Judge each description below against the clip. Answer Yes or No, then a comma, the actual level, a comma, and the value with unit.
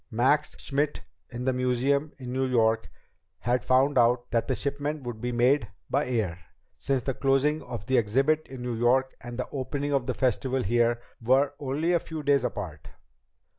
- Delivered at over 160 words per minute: Yes, average, 180 wpm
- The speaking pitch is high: No, low, 130 Hz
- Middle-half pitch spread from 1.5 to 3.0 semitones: Yes, narrow, 2.6 semitones